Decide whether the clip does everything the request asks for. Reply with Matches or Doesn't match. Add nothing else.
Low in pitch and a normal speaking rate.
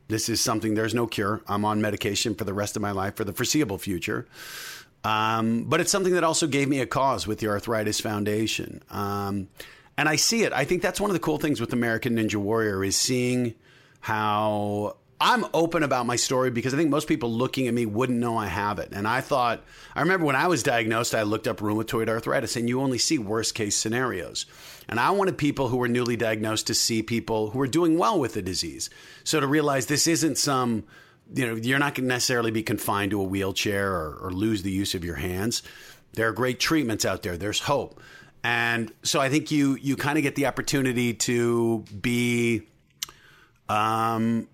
Doesn't match